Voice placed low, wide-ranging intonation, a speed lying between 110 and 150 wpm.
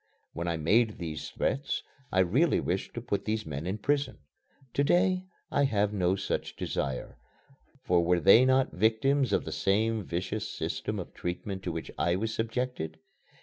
No: low, 105 Hz; wide, 6.2 semitones; average, 170 wpm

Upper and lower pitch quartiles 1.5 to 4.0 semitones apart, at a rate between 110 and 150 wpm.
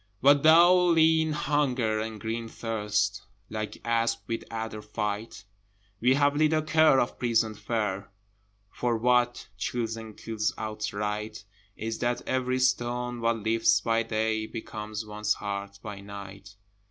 Yes: narrow, 2.5 semitones; slow, 135 wpm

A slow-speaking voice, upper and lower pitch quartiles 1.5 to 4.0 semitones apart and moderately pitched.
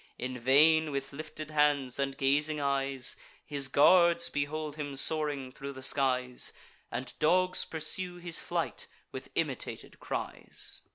Yes: slow, 130 wpm; narrow, 2.5 semitones; medium, 145 Hz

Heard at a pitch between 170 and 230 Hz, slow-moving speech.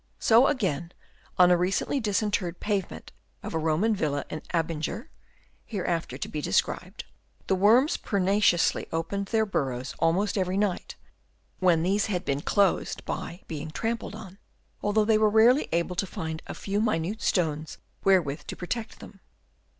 No: high, 190 Hz; average, 155 wpm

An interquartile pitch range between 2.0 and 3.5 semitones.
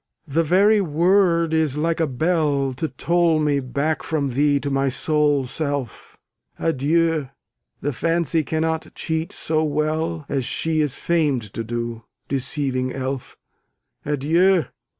Yes: average, 3.0 semitones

